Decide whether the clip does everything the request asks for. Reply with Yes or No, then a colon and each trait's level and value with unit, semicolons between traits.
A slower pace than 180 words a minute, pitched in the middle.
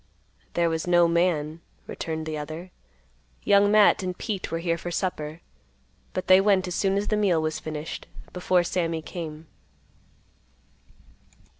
Yes: average, 145 wpm; medium, 170 Hz